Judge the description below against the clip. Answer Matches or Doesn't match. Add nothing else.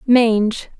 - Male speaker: Doesn't match